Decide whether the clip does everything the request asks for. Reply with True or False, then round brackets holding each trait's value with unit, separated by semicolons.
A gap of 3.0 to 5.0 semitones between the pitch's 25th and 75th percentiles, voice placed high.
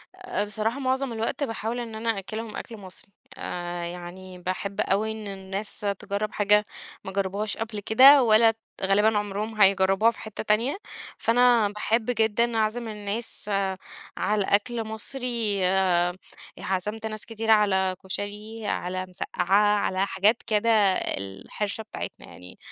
False (2.5 semitones; 210 Hz)